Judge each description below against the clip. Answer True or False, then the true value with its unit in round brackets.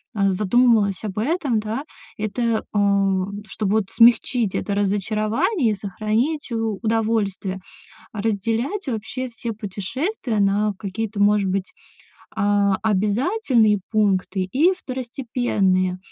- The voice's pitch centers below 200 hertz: False (215 Hz)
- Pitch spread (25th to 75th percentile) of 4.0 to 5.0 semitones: False (3.0 semitones)